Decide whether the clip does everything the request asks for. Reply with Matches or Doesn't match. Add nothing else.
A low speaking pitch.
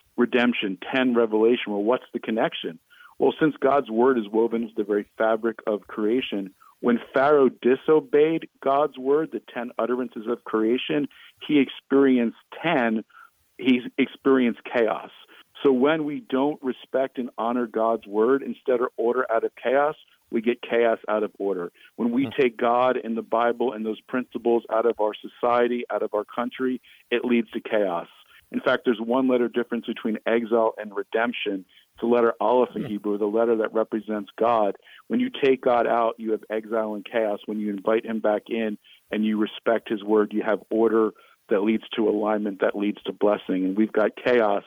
Matches